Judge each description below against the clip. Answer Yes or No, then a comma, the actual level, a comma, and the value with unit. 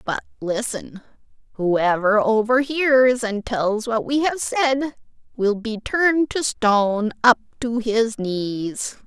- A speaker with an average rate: No, slow, 125 wpm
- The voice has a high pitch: Yes, high, 230 Hz